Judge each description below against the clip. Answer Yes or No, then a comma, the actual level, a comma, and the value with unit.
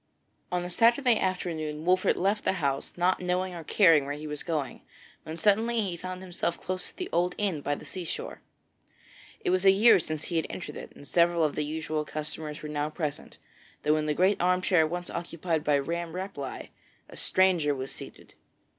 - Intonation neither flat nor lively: Yes, average, 3.4 semitones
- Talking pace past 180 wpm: Yes, average, 200 wpm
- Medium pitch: Yes, medium, 170 Hz